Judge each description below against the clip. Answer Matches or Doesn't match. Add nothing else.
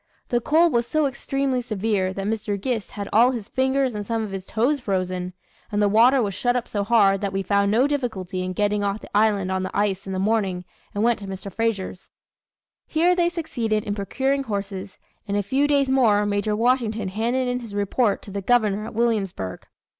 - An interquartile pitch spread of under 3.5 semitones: Doesn't match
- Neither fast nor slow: Doesn't match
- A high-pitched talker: Matches